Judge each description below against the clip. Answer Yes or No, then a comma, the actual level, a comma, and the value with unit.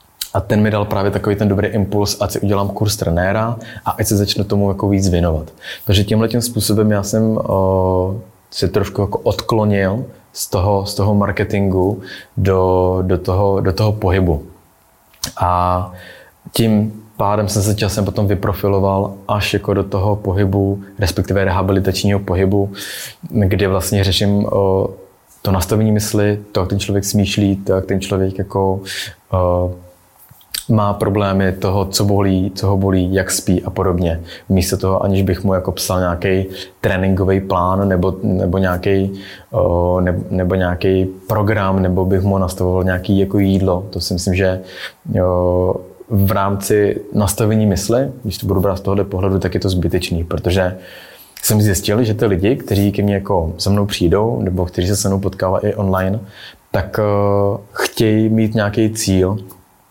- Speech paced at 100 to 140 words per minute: No, average, 155 wpm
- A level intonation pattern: Yes, narrow, 1.6 semitones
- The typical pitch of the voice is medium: No, low, 100 Hz